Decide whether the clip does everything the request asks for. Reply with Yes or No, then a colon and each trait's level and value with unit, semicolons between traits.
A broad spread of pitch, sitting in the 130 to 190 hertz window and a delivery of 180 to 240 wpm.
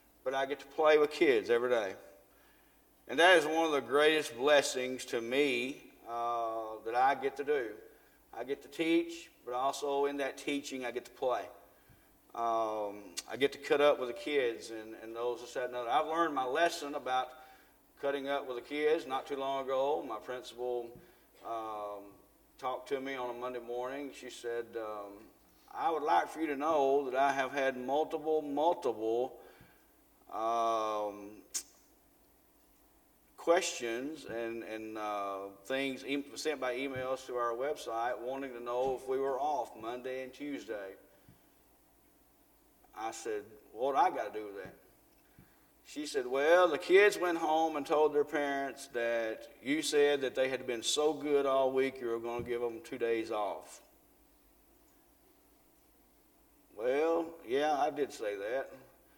No: wide, 5.7 semitones; medium, 140 Hz; average, 165 wpm